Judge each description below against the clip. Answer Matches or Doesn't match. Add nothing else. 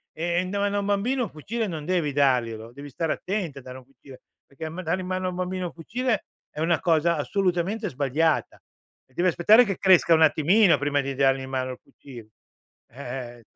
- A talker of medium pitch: Matches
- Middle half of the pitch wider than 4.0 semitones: Matches